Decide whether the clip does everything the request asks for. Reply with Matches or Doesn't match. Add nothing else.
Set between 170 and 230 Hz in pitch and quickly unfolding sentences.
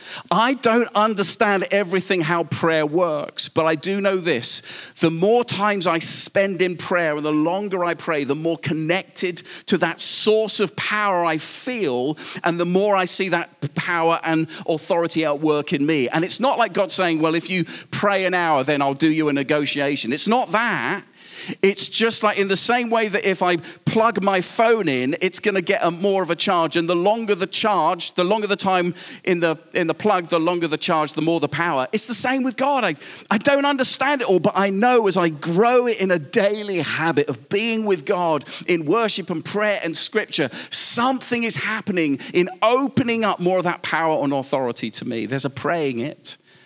Matches